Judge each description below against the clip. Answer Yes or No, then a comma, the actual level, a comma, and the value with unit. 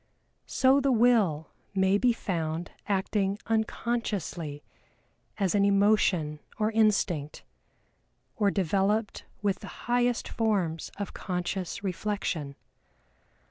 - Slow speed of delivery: Yes, slow, 100 wpm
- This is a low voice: No, high, 200 Hz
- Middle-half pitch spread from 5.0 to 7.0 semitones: No, average, 3.8 semitones